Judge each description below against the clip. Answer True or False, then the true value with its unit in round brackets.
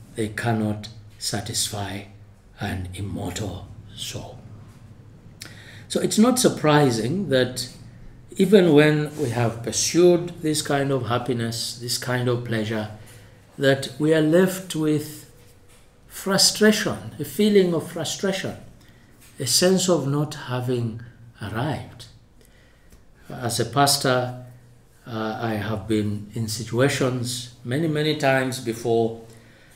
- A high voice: False (120 Hz)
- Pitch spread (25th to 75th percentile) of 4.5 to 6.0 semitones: True (5.1 semitones)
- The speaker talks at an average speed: False (105 wpm)